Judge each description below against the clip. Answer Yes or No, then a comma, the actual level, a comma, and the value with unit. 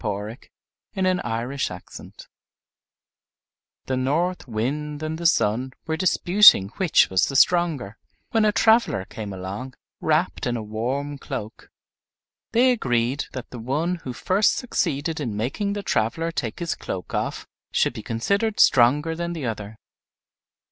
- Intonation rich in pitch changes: Yes, wide, 7.2 semitones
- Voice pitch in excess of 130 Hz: Yes, medium, 140 Hz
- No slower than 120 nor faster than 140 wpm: Yes, slow, 135 wpm